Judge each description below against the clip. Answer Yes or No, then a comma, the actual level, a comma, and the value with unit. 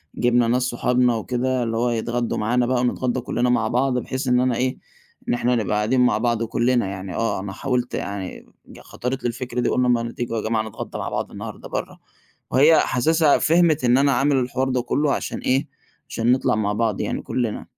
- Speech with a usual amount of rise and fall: No, narrow, 1.9 semitones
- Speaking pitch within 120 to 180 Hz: Yes, low, 125 Hz